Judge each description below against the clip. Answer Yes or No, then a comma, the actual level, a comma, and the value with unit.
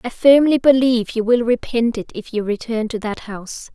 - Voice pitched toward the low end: No, high, 230 Hz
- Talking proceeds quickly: Yes, fast, 210 wpm